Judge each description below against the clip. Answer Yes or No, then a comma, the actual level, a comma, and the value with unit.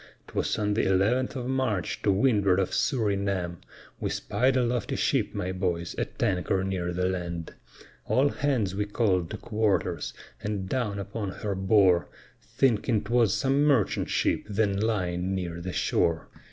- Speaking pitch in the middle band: No, low, 100 Hz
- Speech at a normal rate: Yes, average, 155 wpm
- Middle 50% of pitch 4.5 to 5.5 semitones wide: No, average, 3.7 semitones